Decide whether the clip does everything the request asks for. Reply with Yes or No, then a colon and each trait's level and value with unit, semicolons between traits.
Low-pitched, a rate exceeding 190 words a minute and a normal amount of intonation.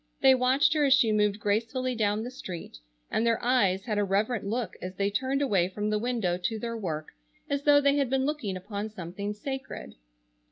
No: high, 220 Hz; fast, 205 wpm; average, 4.4 semitones